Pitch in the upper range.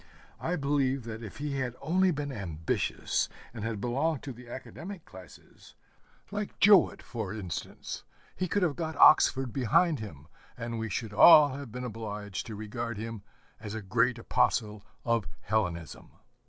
No: low, 120 Hz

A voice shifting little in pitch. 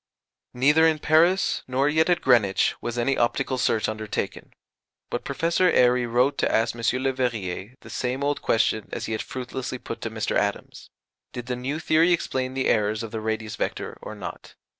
No: average, 4.0 semitones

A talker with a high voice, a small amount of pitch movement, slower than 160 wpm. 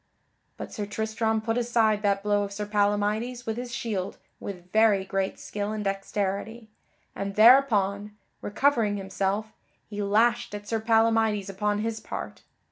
Yes: high, 210 Hz; narrow, 1.8 semitones; average, 145 wpm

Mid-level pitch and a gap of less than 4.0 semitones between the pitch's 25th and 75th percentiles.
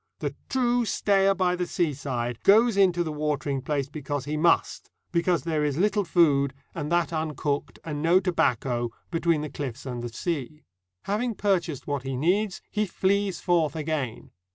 No: medium, 160 Hz; average, 4.5 semitones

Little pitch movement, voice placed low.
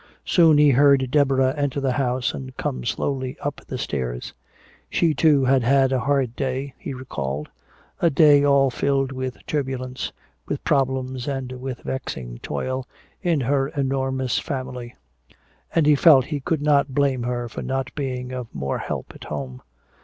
Yes: narrow, 1.9 semitones; low, 130 Hz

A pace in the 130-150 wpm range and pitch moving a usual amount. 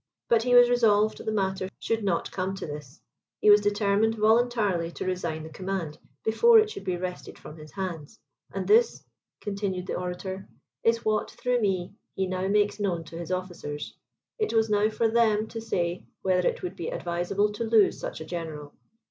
No: average, 190 wpm; average, 3.8 semitones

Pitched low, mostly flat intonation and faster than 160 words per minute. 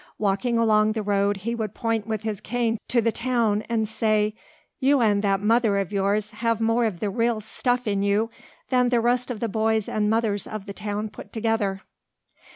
No: high, 220 Hz; narrow, 2.0 semitones; average, 200 wpm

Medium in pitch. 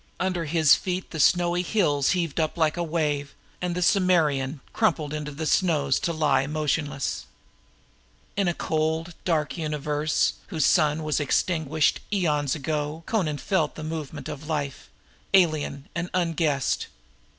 Yes: medium, 155 Hz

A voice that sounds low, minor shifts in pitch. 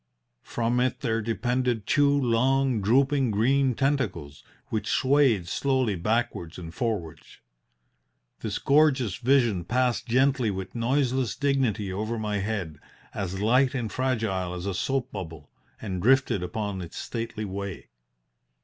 No: low, 115 Hz; average, 5.0 semitones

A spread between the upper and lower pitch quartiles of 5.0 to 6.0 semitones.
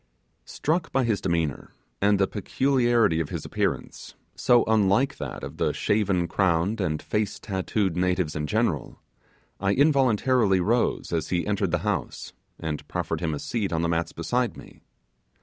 Yes: wide, 5.6 semitones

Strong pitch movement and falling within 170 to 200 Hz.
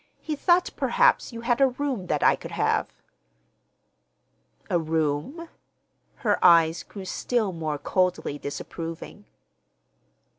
Yes: wide, 8.3 semitones; medium, 185 Hz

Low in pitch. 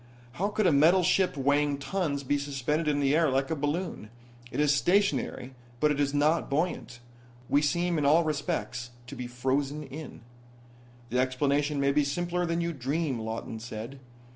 No: medium, 145 Hz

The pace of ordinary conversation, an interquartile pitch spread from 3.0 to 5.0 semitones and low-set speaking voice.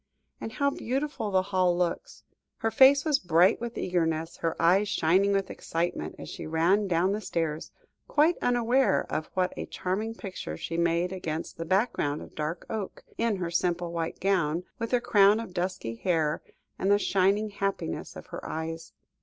No: average, 175 wpm; average, 4.1 semitones; medium, 185 Hz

